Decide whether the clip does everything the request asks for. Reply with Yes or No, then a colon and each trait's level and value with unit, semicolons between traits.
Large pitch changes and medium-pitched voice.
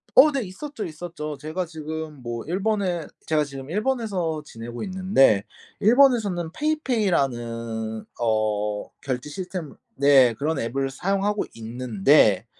Yes: wide, 8.3 semitones; medium, 155 Hz